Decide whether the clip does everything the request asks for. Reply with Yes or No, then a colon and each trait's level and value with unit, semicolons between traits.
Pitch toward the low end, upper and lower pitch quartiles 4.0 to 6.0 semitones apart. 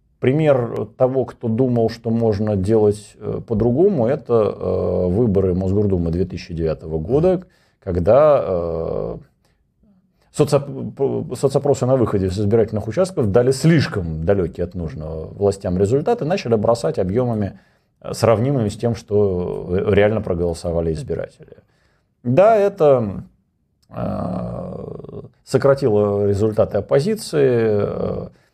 Yes: low, 110 Hz; wide, 5.5 semitones